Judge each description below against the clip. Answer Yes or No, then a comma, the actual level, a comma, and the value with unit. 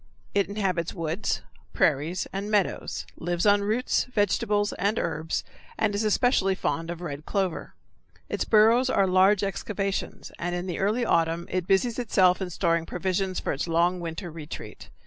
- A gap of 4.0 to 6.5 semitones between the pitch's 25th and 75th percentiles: No, average, 3.3 semitones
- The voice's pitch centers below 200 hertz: Yes, high, 190 Hz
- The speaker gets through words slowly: No, average, 160 wpm